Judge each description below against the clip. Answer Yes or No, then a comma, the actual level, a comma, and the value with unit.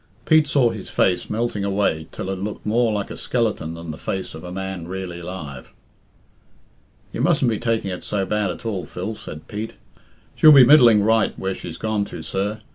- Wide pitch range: No, average, 3.7 semitones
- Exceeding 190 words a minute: Yes, average, 200 wpm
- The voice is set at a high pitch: No, low, 100 Hz